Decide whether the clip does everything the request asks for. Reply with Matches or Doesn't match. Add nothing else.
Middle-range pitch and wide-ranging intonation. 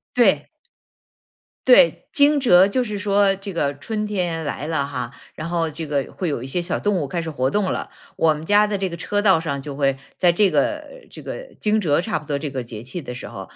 Matches